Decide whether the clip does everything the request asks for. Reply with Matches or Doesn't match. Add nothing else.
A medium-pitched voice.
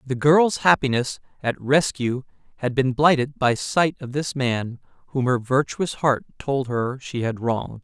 Doesn't match